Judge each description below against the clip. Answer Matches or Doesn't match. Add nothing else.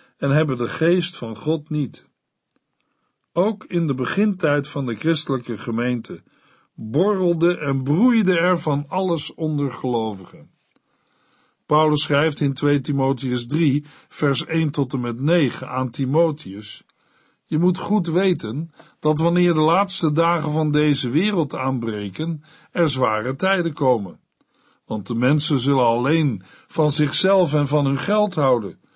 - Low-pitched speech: Doesn't match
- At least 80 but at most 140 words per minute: Matches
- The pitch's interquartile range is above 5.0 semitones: Doesn't match